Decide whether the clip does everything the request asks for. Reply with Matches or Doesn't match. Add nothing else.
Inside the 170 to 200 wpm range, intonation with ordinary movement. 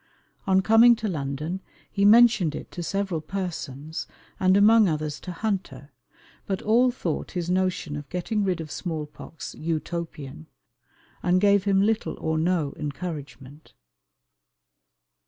Doesn't match